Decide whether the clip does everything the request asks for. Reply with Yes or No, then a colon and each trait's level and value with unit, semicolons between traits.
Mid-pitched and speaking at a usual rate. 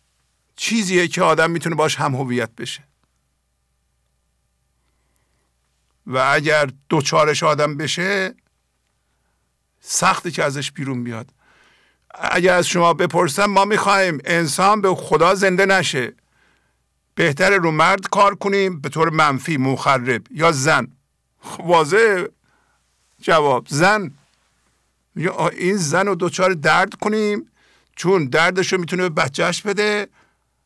No: medium, 155 Hz; slow, 110 wpm